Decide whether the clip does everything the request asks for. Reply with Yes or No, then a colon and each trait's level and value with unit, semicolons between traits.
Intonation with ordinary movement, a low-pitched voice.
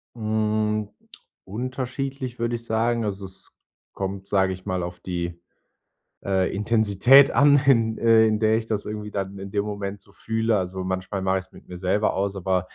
Yes: average, 3.0 semitones; low, 105 Hz